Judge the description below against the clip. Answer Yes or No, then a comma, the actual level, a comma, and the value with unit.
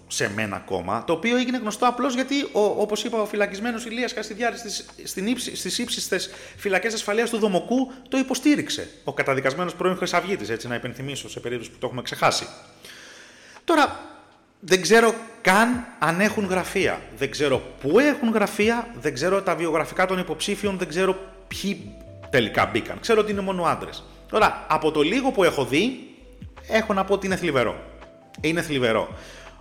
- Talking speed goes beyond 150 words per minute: Yes, average, 160 wpm